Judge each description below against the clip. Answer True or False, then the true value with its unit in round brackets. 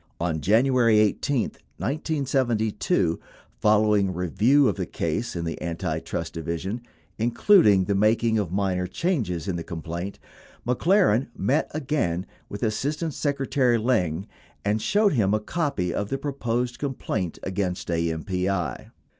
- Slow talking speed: True (125 wpm)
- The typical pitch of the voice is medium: False (105 Hz)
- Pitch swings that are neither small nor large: False (6.3 semitones)